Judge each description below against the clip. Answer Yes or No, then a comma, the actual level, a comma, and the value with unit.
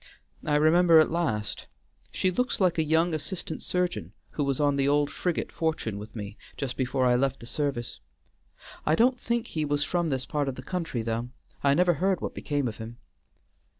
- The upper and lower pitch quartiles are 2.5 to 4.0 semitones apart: No, average, 4.9 semitones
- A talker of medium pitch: Yes, medium, 145 Hz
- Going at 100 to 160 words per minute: No, average, 195 wpm